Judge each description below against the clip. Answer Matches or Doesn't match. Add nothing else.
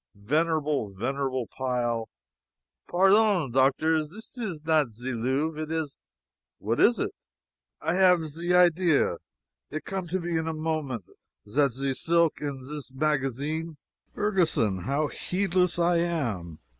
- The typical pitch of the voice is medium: Matches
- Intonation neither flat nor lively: Matches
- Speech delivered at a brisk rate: Doesn't match